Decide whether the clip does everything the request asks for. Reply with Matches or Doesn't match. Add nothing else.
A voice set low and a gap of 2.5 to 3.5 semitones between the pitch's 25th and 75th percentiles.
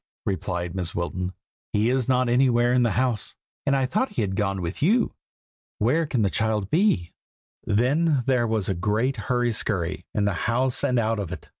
Doesn't match